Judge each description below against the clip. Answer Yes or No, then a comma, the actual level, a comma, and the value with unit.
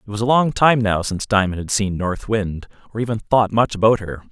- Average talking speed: No, fast, 250 wpm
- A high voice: No, low, 105 Hz